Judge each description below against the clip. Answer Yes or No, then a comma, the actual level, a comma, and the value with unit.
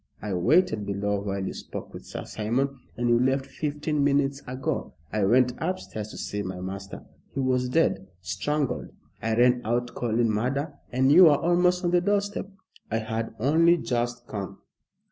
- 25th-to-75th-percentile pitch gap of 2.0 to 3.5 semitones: No, average, 5.3 semitones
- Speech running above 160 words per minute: Yes, average, 170 wpm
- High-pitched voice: No, low, 125 Hz